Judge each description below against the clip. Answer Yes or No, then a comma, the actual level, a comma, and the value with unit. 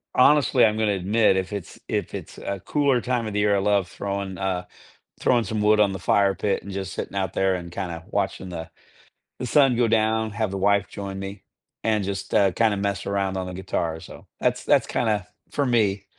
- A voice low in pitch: Yes, low, 100 Hz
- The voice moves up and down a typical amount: No, narrow, 2.3 semitones